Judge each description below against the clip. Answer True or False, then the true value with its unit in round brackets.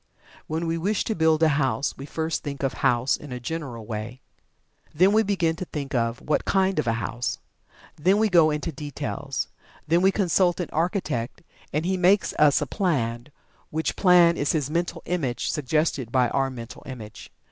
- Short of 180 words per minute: False (185 wpm)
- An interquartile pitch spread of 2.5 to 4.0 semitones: False (5.1 semitones)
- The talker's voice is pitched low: False (155 Hz)